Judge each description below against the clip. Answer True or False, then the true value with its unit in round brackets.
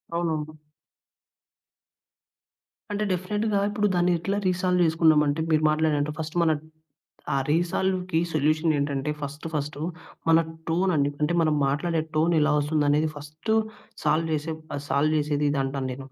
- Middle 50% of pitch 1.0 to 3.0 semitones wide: True (2.7 semitones)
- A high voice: False (155 Hz)